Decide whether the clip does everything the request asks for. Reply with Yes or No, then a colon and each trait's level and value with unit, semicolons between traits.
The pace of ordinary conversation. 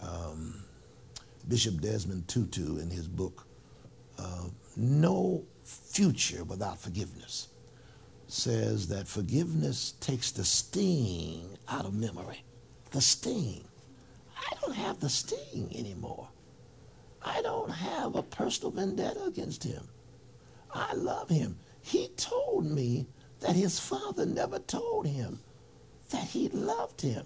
No: slow, 115 wpm